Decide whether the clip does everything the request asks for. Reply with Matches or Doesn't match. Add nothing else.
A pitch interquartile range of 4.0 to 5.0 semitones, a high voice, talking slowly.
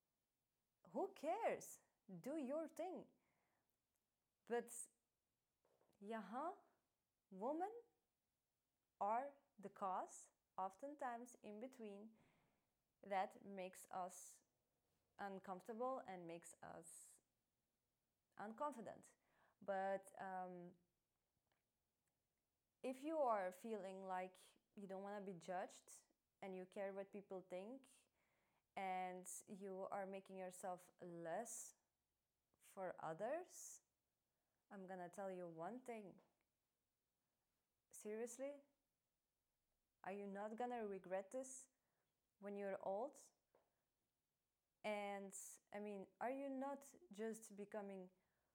Matches